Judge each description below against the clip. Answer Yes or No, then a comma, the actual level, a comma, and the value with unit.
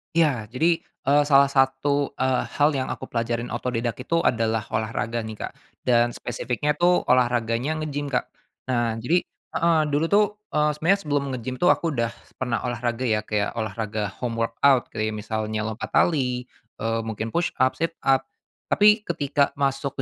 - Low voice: Yes, low, 125 Hz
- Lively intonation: No, average, 4.2 semitones